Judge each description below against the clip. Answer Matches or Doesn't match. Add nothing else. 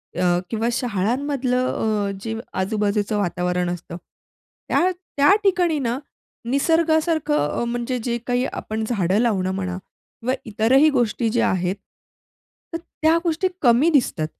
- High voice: Matches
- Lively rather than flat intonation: Matches